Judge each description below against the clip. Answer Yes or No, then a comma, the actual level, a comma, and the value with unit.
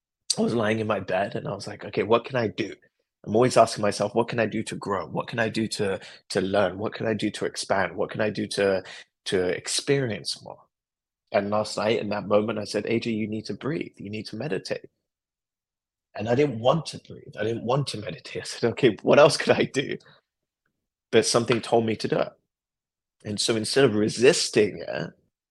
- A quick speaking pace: Yes, fast, 225 wpm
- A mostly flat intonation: Yes, narrow, 1.7 semitones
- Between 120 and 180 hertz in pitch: No, low, 110 Hz